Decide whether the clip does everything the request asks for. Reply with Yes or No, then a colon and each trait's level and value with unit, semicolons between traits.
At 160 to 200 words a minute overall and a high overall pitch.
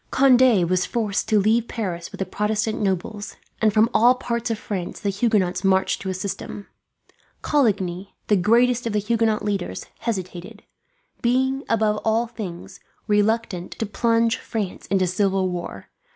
No: average, 150 wpm; high, 210 Hz